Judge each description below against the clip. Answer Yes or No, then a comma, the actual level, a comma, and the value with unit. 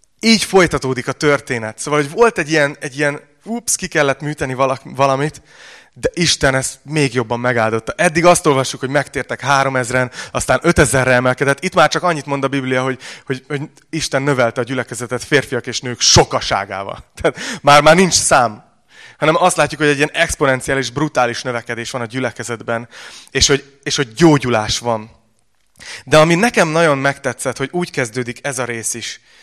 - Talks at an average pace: No, fast, 175 wpm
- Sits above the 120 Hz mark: Yes, low, 135 Hz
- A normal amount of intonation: Yes, average, 3.3 semitones